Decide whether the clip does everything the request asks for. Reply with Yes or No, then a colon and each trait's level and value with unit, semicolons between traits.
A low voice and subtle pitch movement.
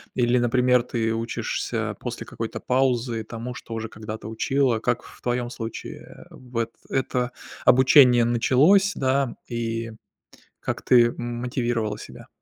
Yes: low, 120 Hz; narrow, 1.7 semitones